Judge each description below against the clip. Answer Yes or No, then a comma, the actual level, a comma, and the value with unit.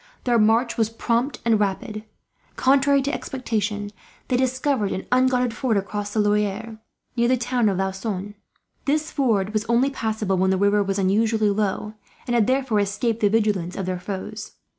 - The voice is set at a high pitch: Yes, high, 215 Hz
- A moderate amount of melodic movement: Yes, average, 3.3 semitones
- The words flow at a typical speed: Yes, average, 170 wpm